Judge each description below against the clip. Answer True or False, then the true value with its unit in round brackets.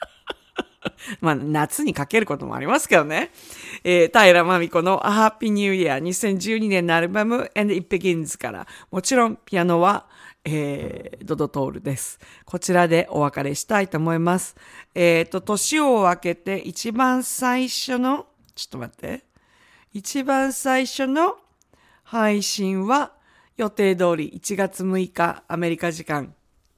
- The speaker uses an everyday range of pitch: True (4.9 semitones)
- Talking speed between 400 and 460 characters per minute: False (285 characters per minute)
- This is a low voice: False (190 Hz)